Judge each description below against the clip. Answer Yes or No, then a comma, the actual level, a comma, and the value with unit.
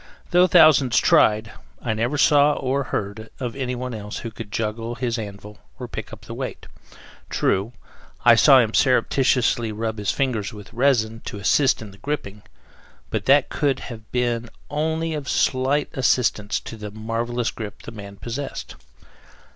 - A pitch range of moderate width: Yes, average, 3.7 semitones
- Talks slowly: No, average, 160 wpm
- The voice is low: Yes, low, 120 Hz